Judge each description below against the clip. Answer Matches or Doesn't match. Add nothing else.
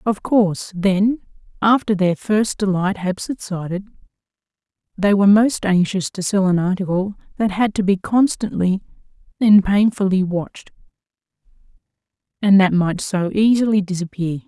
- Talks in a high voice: Matches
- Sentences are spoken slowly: Matches